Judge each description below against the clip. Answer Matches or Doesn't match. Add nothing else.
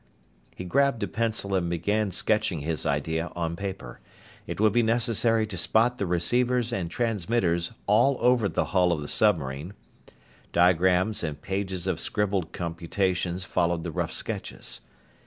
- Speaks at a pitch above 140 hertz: Doesn't match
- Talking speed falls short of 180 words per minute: Matches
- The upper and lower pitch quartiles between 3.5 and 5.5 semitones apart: Matches